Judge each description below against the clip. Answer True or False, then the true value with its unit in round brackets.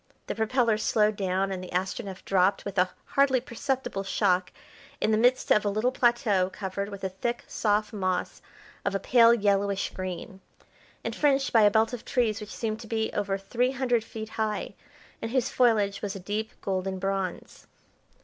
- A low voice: False (210 Hz)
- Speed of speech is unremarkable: True (180 wpm)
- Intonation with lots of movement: False (3.3 semitones)